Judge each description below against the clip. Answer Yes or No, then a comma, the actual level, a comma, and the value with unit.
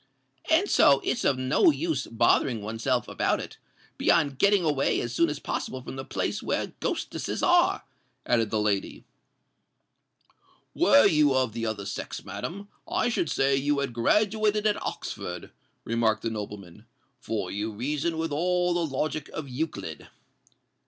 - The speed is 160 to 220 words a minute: No, average, 150 wpm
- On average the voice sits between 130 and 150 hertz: Yes, low, 135 Hz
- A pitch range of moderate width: No, wide, 6.5 semitones